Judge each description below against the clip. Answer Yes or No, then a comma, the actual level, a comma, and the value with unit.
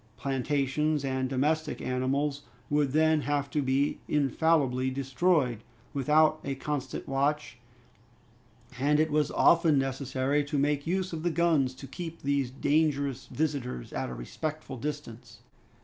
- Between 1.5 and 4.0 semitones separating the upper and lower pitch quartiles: Yes, narrow, 2.5 semitones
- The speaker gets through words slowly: Yes, slow, 130 wpm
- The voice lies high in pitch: No, medium, 140 Hz